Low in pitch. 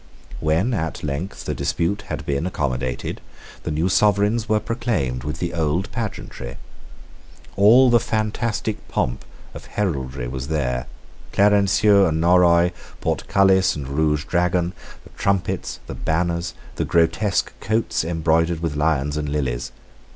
Yes: very low, 85 Hz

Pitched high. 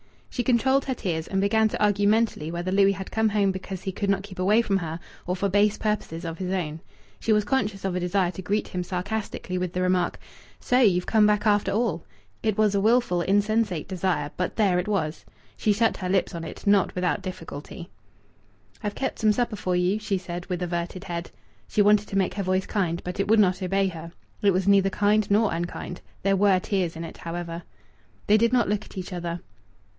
Yes: high, 195 Hz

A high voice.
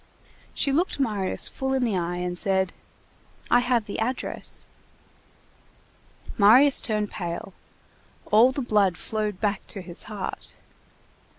Yes: high, 210 Hz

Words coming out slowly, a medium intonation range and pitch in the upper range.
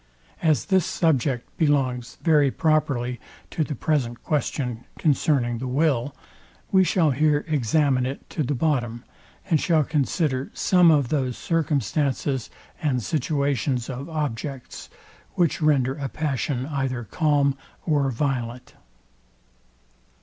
No: slow, 120 wpm; average, 3.5 semitones; medium, 140 Hz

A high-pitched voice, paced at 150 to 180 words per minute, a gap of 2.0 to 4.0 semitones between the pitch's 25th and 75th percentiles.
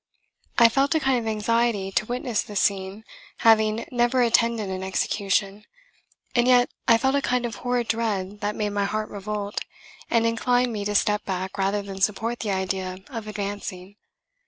Yes: high, 215 Hz; average, 175 wpm; average, 2.9 semitones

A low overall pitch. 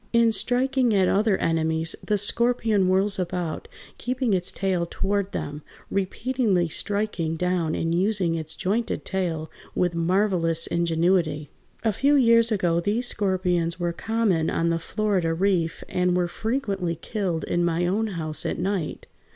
No: medium, 185 Hz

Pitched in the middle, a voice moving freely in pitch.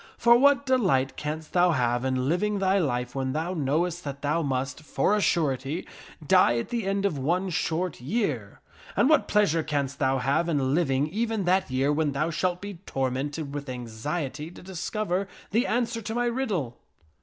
Yes: medium, 160 Hz; wide, 6.2 semitones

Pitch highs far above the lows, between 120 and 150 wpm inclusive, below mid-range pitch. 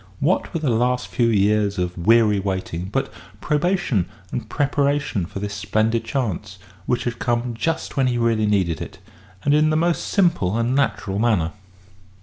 No: wide, 5.7 semitones; average, 165 wpm; low, 115 Hz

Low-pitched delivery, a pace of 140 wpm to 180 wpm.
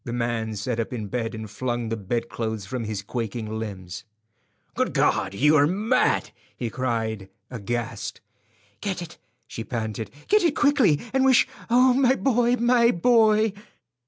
Yes: low, 120 Hz; average, 150 wpm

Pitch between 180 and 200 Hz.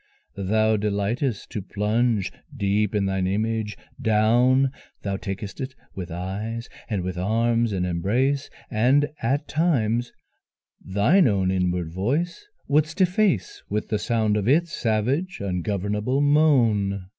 No: low, 110 Hz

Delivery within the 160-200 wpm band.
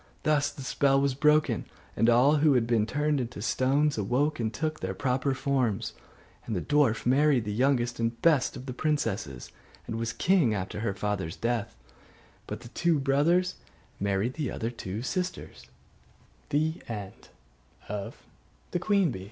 No: average, 145 wpm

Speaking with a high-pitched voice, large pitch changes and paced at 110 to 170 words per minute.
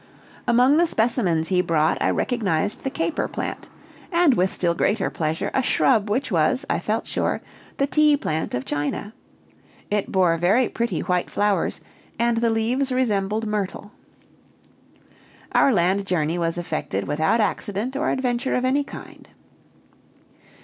Yes: high, 210 Hz; wide, 6.4 semitones; average, 145 wpm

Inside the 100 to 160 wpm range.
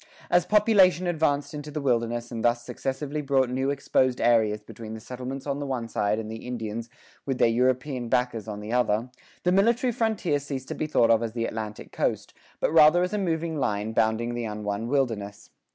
No: average, 200 wpm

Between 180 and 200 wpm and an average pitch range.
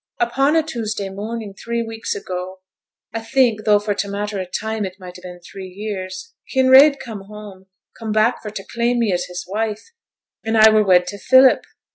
Yes: average, 195 wpm; average, 3.3 semitones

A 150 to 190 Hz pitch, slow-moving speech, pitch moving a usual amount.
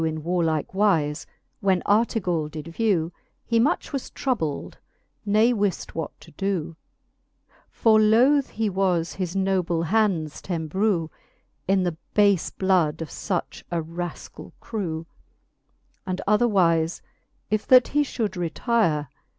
Yes: medium, 185 Hz; slow, 125 wpm; average, 4.6 semitones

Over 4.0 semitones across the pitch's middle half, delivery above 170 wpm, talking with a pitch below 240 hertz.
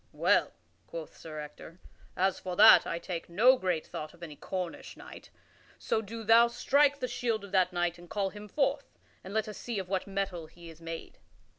Yes: average, 4.5 semitones; average, 200 wpm; high, 190 Hz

